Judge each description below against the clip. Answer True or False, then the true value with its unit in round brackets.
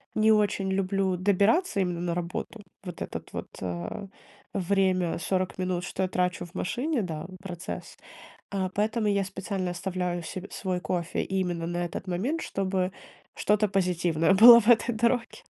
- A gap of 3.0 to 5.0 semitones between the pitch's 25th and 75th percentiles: False (2.4 semitones)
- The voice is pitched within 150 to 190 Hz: True (185 Hz)